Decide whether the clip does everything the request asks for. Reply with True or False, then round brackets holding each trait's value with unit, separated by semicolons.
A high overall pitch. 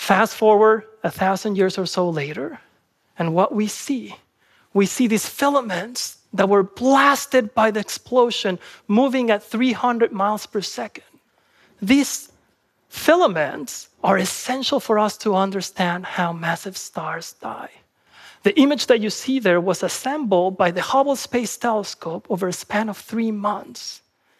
True (215 Hz)